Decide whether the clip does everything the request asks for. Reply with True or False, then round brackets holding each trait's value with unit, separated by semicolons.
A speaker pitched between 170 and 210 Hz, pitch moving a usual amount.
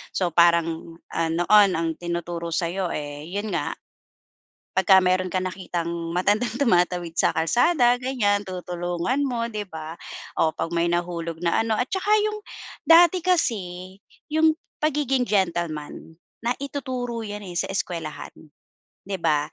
False (185 Hz; 5.8 semitones)